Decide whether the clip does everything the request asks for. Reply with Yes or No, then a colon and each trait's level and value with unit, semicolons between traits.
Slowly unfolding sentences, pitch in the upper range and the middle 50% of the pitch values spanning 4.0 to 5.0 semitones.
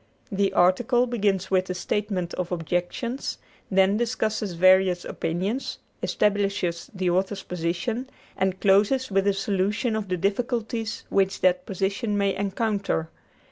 No: slow, 130 wpm; high, 195 Hz; average, 2.7 semitones